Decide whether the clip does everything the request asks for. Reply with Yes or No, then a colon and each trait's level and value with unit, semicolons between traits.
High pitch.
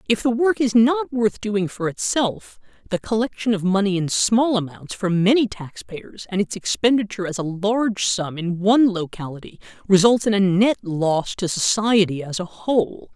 Yes: high, 200 Hz